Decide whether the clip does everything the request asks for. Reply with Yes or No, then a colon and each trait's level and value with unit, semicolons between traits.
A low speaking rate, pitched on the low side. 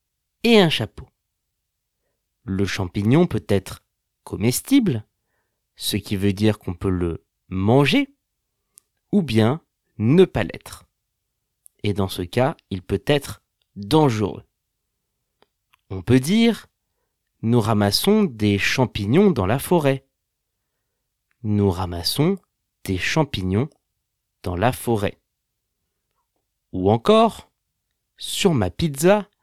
Yes: slow, 105 wpm; low, 110 Hz